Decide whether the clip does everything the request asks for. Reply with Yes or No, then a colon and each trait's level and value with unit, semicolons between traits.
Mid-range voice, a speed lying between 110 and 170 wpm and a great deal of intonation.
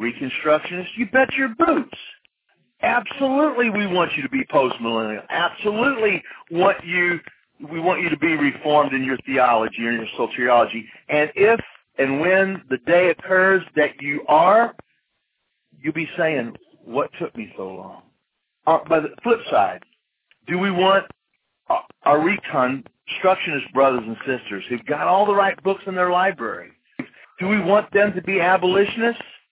Yes: medium, 180 Hz; average, 150 wpm; wide, 6.2 semitones